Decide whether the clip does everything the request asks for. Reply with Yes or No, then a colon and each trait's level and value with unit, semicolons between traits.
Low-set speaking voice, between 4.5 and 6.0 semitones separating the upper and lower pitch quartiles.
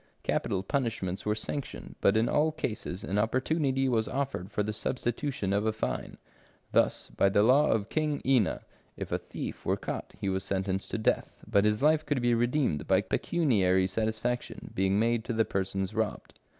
Yes: low, 110 Hz; average, 5.0 semitones